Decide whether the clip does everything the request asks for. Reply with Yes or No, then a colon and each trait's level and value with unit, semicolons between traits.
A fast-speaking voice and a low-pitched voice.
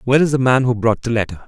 Yes: fast, 325 wpm; low, 120 Hz